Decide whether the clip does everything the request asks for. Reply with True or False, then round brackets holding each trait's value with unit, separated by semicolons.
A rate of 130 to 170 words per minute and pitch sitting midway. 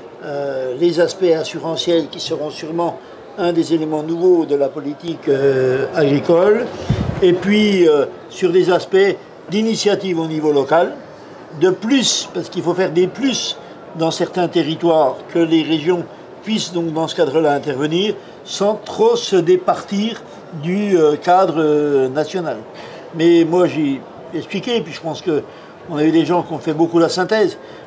True (160 wpm; 170 Hz)